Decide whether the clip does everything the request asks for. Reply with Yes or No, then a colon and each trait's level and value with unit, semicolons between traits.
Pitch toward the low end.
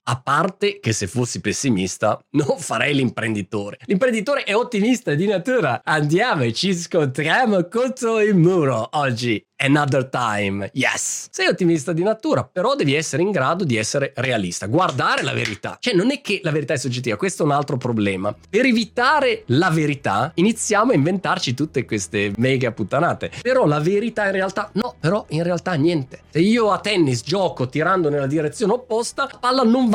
No: medium, 160 Hz